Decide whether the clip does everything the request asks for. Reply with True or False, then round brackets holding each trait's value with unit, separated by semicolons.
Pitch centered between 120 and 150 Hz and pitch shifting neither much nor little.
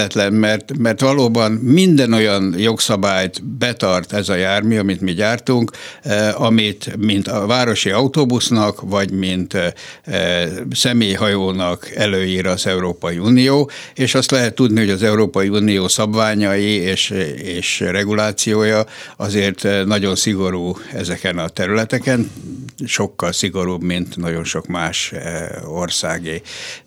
False (105 Hz; 3.1 semitones)